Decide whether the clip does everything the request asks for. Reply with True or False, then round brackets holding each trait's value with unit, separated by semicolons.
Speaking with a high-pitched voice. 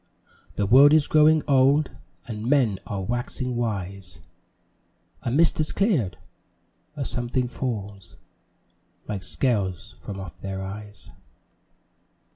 False (120 Hz)